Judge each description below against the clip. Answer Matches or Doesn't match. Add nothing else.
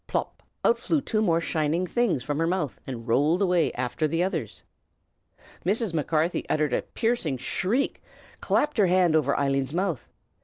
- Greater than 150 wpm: Matches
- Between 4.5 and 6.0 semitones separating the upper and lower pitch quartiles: Matches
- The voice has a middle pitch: Matches